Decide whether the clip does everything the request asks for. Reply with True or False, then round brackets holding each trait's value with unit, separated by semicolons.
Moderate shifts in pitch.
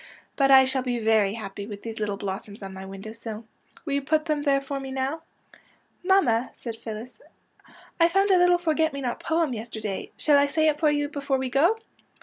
False (5.7 semitones)